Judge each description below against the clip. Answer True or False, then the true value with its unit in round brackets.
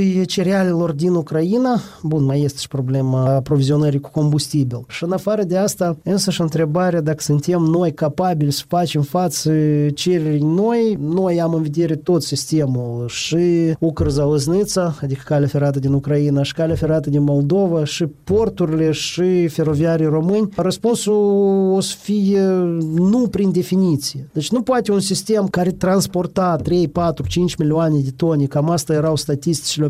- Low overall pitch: False (165 Hz)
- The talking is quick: False (150 wpm)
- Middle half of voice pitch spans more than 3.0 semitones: True (3.8 semitones)